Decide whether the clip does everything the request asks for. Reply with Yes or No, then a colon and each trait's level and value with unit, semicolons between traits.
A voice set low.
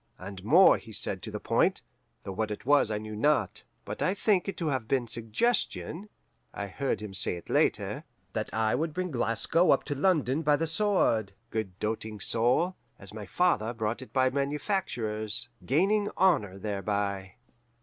Yes: low, 120 Hz